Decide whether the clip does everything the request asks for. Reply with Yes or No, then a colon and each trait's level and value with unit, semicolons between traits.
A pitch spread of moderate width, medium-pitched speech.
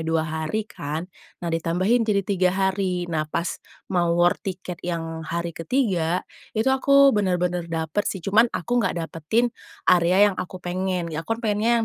Yes: average, 3.7 semitones; medium, 180 Hz